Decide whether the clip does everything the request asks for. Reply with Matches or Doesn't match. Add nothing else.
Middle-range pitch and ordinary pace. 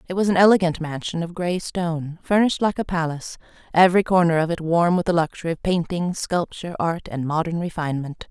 Matches